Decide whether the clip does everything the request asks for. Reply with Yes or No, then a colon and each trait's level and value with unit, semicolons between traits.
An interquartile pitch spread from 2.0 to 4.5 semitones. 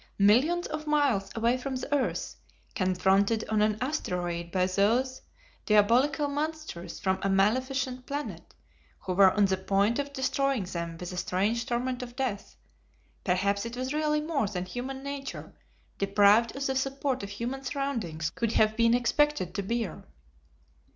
No: wide, 5.5 semitones